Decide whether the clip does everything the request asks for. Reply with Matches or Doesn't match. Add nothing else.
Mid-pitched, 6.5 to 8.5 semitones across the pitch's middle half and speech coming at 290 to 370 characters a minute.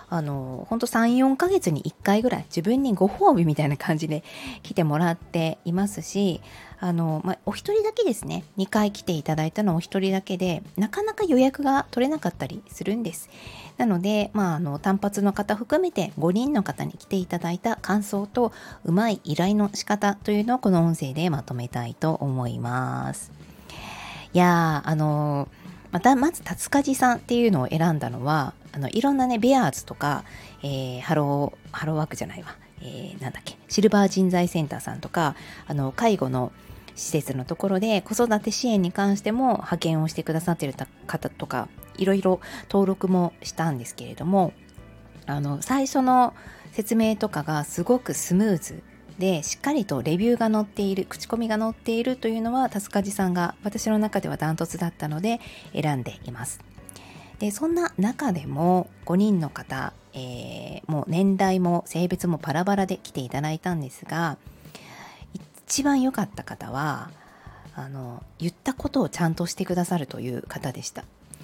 Doesn't match